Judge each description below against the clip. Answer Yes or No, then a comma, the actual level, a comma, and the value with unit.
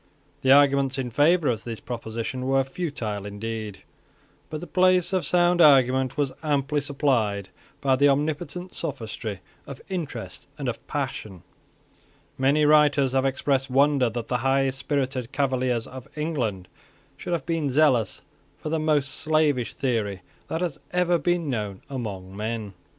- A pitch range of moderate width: Yes, average, 4.4 semitones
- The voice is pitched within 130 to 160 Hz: Yes, low, 135 Hz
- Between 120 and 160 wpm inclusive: Yes, average, 145 wpm